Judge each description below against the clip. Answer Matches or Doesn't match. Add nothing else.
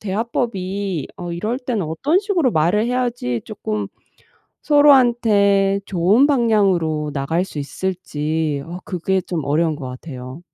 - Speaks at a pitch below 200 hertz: Matches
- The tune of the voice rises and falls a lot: Matches